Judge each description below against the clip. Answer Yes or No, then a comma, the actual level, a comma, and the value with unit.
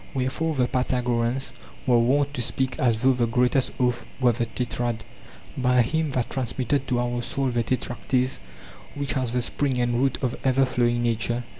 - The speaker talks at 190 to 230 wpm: No, average, 175 wpm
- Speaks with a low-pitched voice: Yes, low, 125 Hz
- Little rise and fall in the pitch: Yes, narrow, 1.6 semitones